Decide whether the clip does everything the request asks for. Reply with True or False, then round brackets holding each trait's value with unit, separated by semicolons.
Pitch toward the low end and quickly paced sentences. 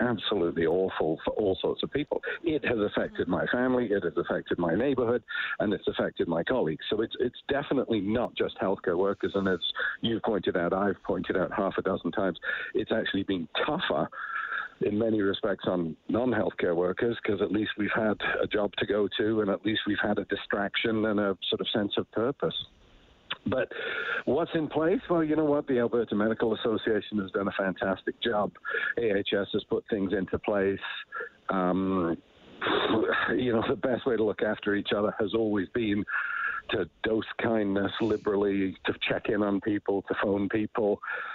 False (105 Hz; 180 wpm)